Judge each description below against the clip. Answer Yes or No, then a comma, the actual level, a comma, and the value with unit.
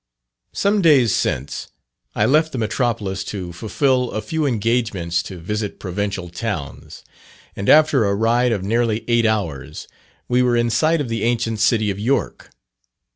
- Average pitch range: Yes, average, 3.8 semitones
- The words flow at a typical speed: Yes, average, 155 wpm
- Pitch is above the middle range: No, low, 115 Hz